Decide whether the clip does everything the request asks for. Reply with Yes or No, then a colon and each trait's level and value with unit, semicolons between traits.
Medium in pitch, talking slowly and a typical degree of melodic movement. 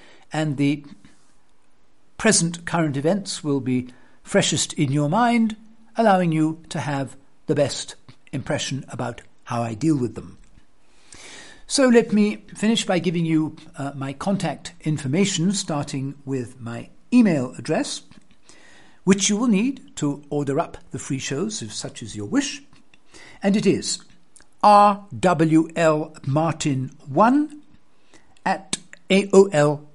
No: medium, 155 Hz; slow, 120 wpm; wide, 6.2 semitones